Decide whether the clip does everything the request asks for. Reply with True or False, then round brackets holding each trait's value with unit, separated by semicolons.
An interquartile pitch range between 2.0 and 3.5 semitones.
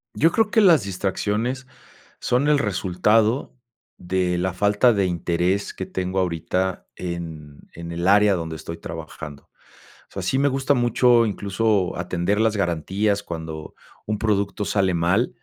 False (4.2 semitones)